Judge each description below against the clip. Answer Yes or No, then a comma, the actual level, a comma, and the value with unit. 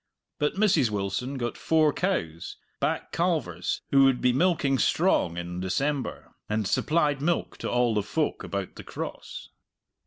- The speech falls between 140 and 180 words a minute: Yes, average, 150 wpm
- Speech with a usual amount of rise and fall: No, wide, 7.5 semitones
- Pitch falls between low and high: No, low, 130 Hz